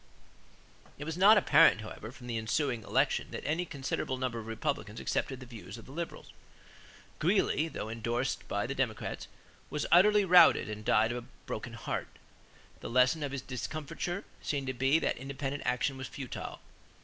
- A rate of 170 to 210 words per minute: Yes, average, 175 wpm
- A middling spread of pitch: Yes, average, 4.3 semitones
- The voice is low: Yes, low, 130 Hz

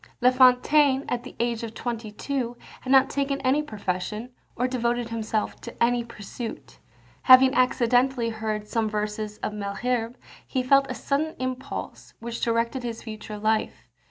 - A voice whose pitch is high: Yes, high, 240 Hz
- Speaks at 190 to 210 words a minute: No, average, 155 wpm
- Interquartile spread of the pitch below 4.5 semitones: Yes, average, 2.7 semitones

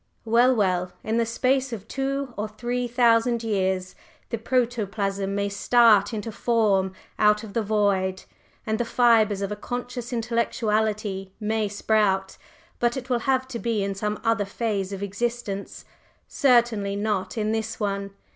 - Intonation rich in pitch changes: No, average, 3.0 semitones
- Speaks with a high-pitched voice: Yes, high, 220 Hz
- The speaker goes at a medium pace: Yes, average, 155 wpm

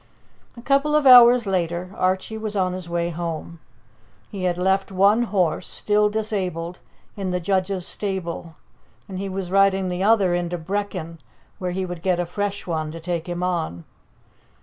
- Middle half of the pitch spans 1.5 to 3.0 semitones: Yes, narrow, 2.6 semitones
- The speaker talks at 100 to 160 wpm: No, average, 170 wpm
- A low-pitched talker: No, medium, 185 Hz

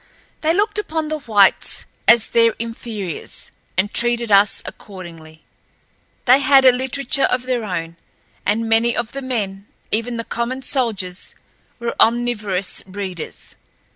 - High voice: Yes, high, 230 Hz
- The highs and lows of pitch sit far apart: No, average, 4.2 semitones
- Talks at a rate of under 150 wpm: Yes, slow, 135 wpm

